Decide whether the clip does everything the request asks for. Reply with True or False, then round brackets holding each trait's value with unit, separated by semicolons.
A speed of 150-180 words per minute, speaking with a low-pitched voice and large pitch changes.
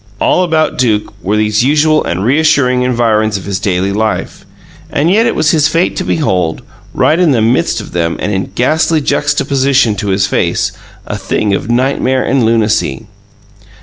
True (175 wpm; 120 Hz; 5.9 semitones)